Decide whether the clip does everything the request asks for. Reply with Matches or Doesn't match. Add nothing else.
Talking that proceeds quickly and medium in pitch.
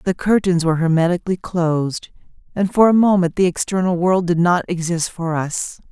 Doesn't match